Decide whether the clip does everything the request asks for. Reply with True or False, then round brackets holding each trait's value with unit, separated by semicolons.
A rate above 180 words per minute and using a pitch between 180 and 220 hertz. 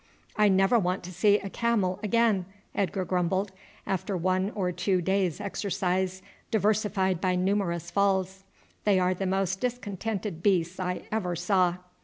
False (145 wpm; 190 Hz)